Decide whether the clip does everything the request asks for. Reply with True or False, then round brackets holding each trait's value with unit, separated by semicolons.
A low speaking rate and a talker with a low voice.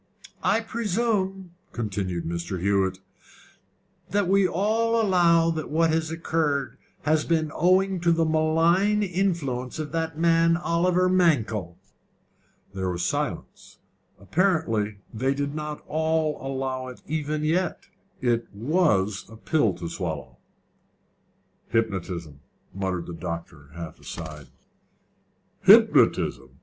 False (115 wpm; 155 Hz)